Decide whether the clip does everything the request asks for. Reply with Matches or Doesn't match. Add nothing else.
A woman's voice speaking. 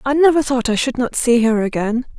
Matches